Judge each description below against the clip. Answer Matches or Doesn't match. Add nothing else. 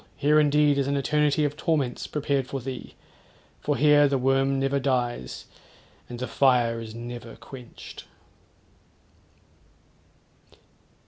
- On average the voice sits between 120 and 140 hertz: Matches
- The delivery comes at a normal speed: Doesn't match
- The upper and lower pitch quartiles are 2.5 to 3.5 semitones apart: Matches